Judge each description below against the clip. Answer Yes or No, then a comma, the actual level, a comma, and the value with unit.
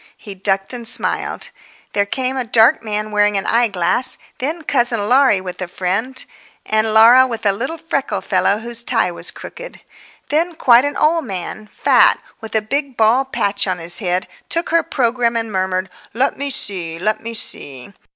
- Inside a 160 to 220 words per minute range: Yes, average, 170 wpm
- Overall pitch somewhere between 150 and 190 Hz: No, high, 225 Hz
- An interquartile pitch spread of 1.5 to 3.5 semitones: No, average, 4.7 semitones